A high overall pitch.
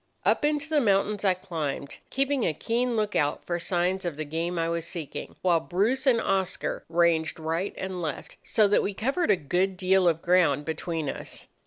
No: medium, 180 Hz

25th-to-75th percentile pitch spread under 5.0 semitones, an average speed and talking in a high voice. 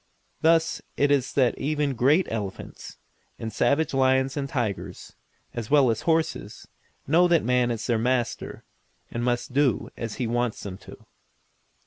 No: average, 3.6 semitones; average, 150 wpm; low, 130 Hz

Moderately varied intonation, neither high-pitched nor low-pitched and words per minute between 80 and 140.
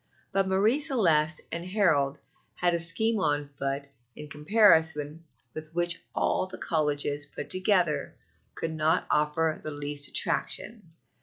Yes: average, 4.0 semitones; medium, 160 Hz; slow, 135 wpm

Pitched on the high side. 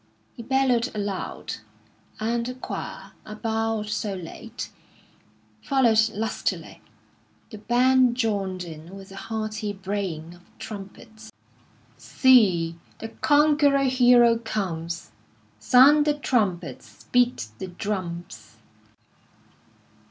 Yes: high, 215 Hz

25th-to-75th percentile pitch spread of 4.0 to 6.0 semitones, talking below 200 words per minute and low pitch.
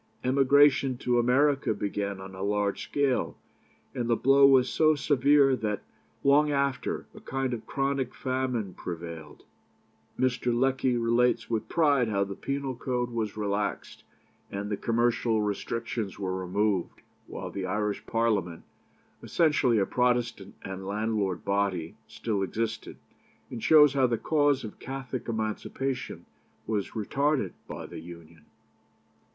Yes: average, 4.7 semitones; slow, 135 wpm; low, 115 Hz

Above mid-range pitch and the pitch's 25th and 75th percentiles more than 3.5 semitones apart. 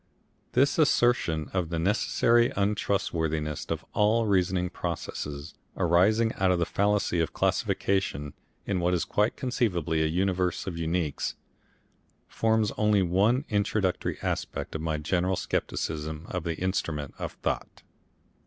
No: very low, 90 Hz; average, 4.2 semitones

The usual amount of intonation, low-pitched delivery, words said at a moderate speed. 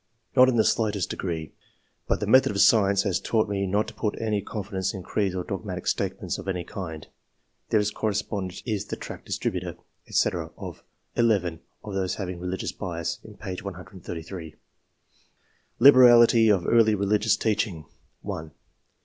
Yes: average, 3.0 semitones; low, 100 Hz; average, 165 wpm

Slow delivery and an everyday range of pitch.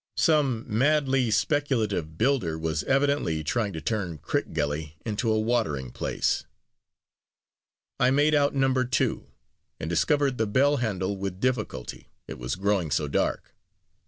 No: slow, 130 wpm; wide, 8.5 semitones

